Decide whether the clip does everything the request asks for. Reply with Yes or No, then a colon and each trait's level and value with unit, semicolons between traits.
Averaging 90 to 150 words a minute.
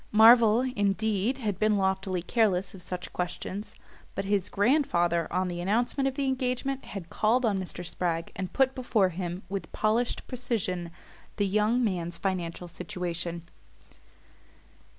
Yes: average, 140 wpm